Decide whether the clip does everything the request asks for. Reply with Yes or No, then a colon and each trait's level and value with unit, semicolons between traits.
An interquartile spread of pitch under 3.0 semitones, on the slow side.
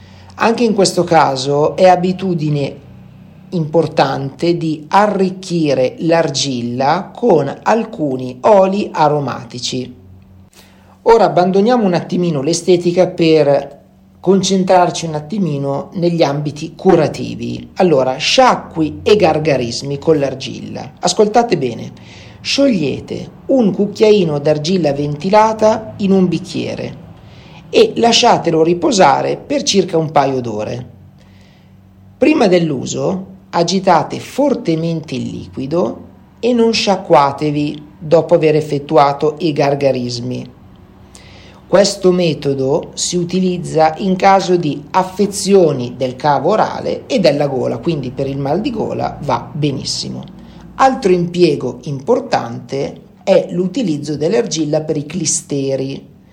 No: average, 5.2 semitones; slow, 100 wpm